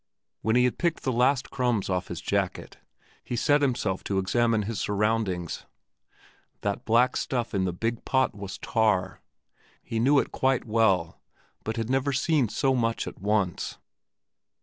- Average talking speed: Yes, average, 160 wpm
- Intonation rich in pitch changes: No, average, 4.0 semitones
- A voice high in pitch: No, low, 115 Hz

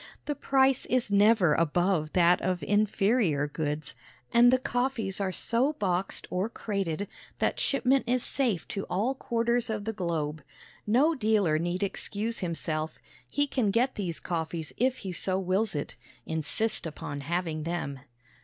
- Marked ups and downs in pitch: Yes, wide, 5.8 semitones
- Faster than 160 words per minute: No, average, 150 wpm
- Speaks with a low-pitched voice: No, high, 195 Hz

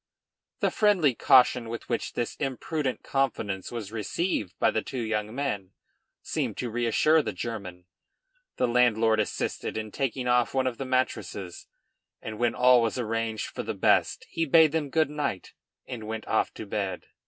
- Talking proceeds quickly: No, average, 165 wpm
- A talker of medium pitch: No, low, 120 Hz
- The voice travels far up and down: No, average, 3.6 semitones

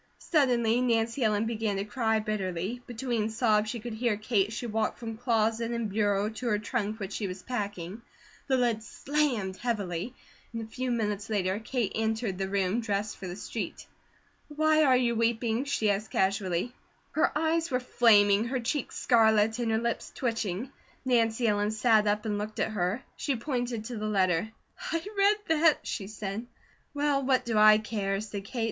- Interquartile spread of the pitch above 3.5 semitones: No, average, 2.9 semitones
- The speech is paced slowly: No, average, 180 wpm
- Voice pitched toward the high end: Yes, high, 220 Hz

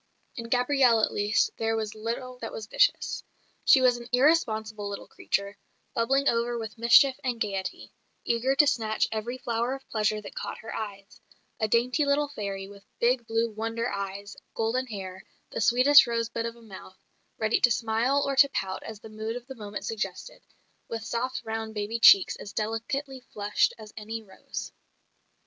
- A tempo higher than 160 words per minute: Yes, average, 175 wpm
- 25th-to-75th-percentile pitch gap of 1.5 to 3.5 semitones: Yes, average, 2.8 semitones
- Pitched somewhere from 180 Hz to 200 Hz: No, high, 230 Hz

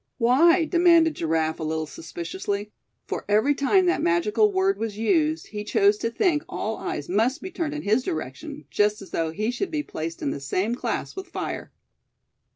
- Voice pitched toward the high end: Yes, high, 230 Hz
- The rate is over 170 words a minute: Yes, average, 185 wpm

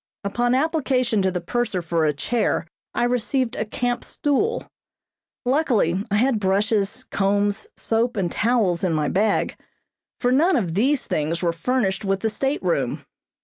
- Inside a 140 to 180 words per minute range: Yes, average, 150 wpm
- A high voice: Yes, high, 220 Hz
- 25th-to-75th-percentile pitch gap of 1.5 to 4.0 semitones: No, average, 4.7 semitones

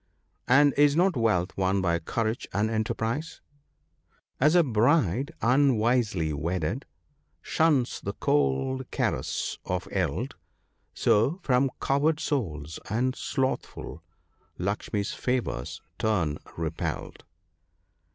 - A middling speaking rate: No, slow, 110 wpm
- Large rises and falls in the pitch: Yes, wide, 6.7 semitones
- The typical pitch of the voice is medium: No, low, 115 Hz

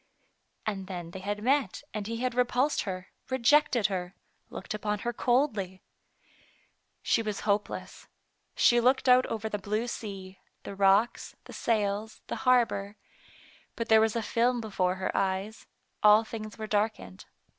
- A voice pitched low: No, high, 215 Hz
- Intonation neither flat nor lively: Yes, average, 3.2 semitones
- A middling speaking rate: Yes, average, 150 wpm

